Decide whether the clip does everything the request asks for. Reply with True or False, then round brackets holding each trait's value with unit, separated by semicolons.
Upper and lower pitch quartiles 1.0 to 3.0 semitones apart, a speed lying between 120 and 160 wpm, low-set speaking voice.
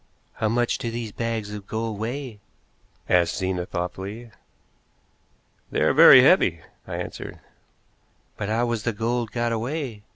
True (2.5 semitones; 140 wpm; 110 Hz)